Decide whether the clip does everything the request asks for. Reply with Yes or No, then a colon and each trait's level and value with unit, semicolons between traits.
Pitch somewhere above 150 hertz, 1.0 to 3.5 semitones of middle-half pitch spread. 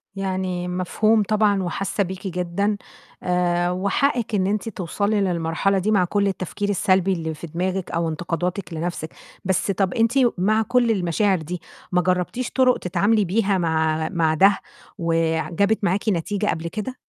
Yes: medium, 185 Hz; average, 2.8 semitones